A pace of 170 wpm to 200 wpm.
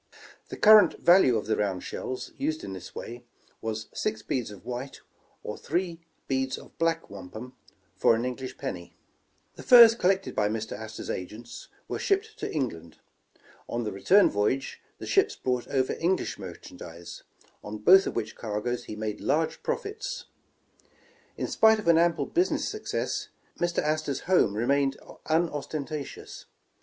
No: average, 155 wpm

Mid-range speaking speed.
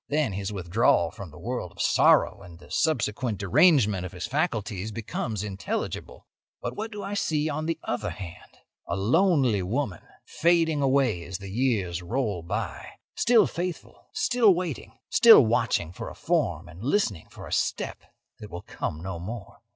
Yes: average, 165 wpm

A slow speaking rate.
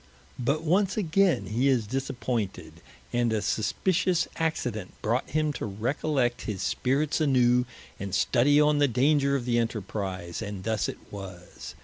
No: average, 145 wpm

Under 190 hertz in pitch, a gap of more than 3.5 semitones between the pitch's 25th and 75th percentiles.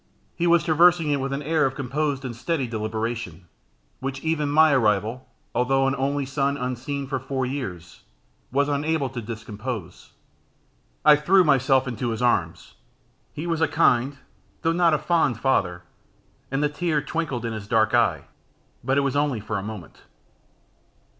Yes: low, 135 Hz; average, 4.2 semitones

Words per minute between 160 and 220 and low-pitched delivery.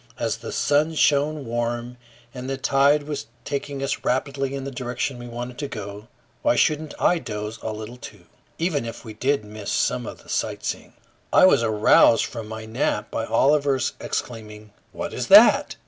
Yes: average, 180 wpm; low, 120 Hz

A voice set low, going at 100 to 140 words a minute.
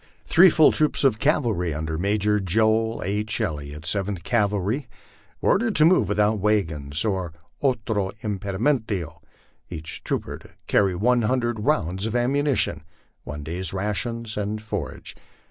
Yes: low, 105 Hz; slow, 135 wpm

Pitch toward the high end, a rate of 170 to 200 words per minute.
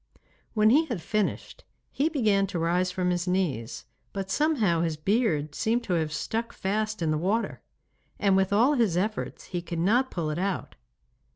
Yes: high, 195 Hz; average, 180 wpm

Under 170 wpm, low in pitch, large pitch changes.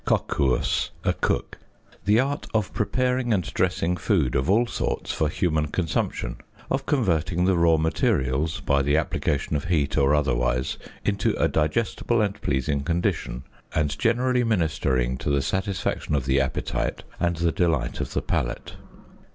Yes: average, 150 wpm; very low, 80 Hz; wide, 6.3 semitones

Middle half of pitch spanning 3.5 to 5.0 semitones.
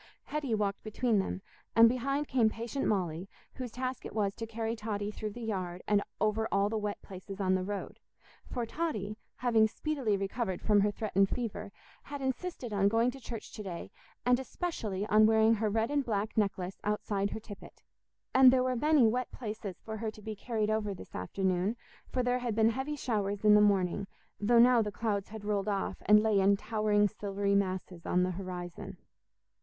No: average, 2.8 semitones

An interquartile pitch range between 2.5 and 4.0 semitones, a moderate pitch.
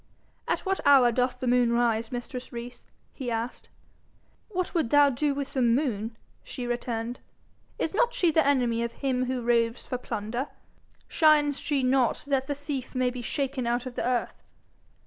No: average, 2.9 semitones; very high, 255 Hz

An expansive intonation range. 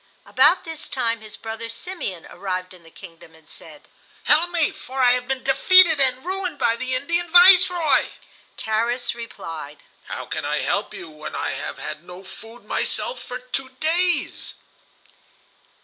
Yes: wide, 8.6 semitones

